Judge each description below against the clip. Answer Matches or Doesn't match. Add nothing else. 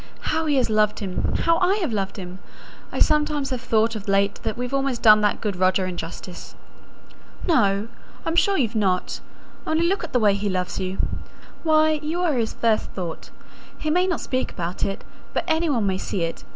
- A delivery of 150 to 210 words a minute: Matches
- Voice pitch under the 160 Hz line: Doesn't match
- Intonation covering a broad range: Matches